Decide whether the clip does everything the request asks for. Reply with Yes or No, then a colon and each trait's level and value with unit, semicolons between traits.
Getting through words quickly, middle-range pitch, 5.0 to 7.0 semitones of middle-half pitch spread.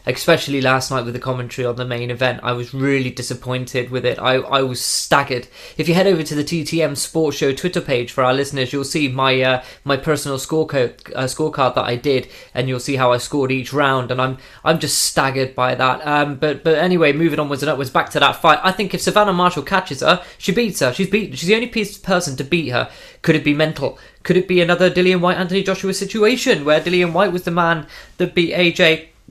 Yes: fast, 235 wpm; medium, 150 Hz; average, 5.3 semitones